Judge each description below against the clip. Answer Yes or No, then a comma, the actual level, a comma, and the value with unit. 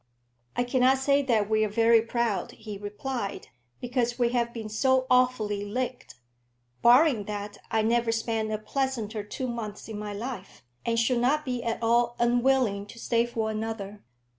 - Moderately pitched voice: No, high, 230 Hz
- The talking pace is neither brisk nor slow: Yes, average, 165 wpm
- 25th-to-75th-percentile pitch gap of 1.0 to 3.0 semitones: Yes, narrow, 2.6 semitones